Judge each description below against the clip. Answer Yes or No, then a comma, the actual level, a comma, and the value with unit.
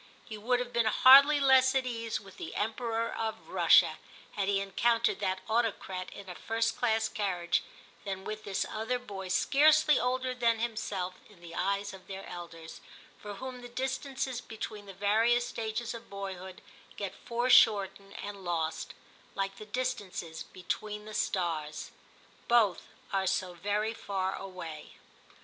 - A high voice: Yes, high, 210 Hz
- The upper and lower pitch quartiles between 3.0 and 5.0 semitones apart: Yes, average, 3.8 semitones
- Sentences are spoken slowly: No, average, 155 wpm